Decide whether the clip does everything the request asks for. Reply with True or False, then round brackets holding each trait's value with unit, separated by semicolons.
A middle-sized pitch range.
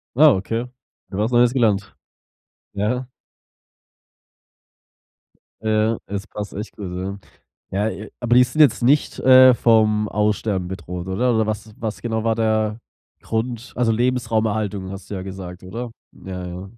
True (3.3 semitones)